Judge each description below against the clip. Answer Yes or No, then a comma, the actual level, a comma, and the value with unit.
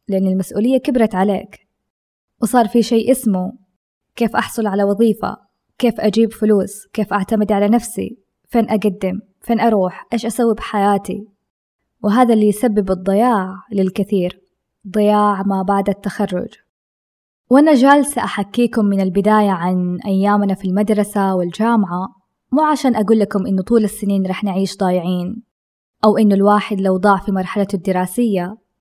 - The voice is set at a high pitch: Yes, high, 205 Hz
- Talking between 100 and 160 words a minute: Yes, average, 130 wpm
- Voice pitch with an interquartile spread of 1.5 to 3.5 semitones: Yes, average, 2.8 semitones